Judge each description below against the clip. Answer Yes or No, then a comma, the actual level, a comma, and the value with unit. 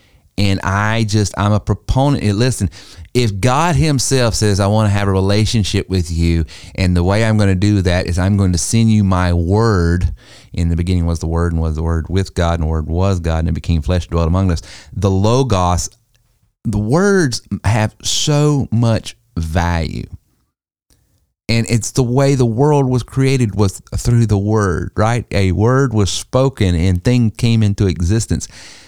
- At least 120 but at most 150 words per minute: No, average, 185 wpm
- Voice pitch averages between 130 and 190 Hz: No, low, 100 Hz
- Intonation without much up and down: No, average, 4.3 semitones